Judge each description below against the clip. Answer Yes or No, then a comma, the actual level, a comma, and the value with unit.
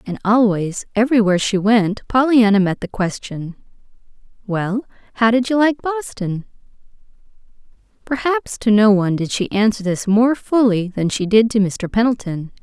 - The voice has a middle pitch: No, high, 215 Hz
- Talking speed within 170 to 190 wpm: No, average, 145 wpm